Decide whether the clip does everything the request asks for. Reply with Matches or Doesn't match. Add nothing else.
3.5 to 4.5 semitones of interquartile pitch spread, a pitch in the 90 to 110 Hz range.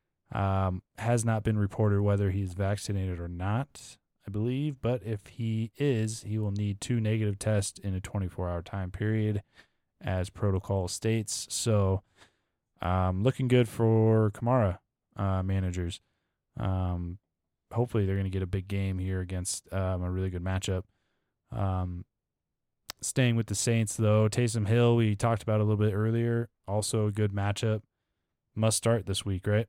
Doesn't match